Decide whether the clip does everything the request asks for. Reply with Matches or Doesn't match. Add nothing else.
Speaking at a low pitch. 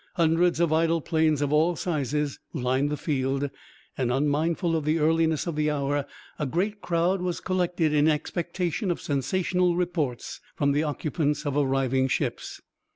Doesn't match